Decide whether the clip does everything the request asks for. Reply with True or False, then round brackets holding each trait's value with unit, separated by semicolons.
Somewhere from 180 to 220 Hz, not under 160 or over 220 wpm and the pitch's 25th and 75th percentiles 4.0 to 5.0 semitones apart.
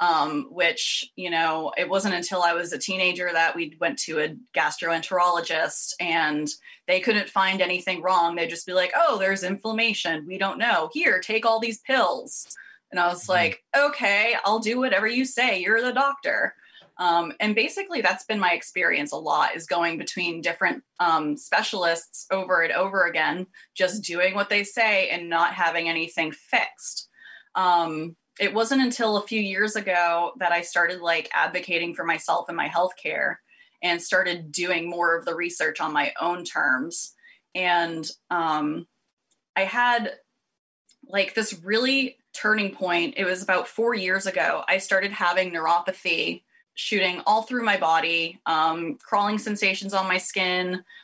True (185 Hz; 165 wpm; 4.3 semitones)